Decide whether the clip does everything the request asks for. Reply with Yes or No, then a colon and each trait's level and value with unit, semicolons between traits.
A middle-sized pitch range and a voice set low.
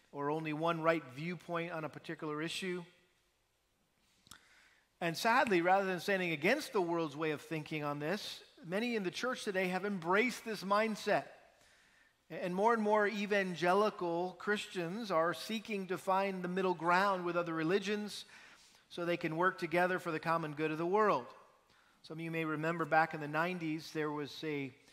No: average, 3.7 semitones; medium, 175 Hz